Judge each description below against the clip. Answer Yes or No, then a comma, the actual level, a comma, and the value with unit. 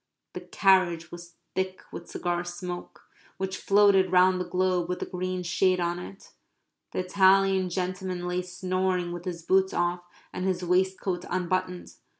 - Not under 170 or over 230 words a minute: No, average, 150 wpm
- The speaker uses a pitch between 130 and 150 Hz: No, medium, 185 Hz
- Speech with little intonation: Yes, narrow, 1.2 semitones